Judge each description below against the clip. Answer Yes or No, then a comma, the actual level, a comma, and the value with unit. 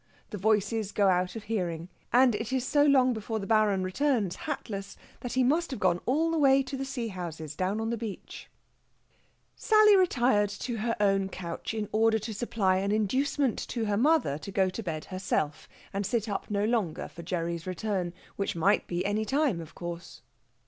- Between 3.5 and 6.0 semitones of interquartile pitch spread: Yes, average, 4.7 semitones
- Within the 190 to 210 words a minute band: Yes, average, 195 wpm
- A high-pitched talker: Yes, high, 210 Hz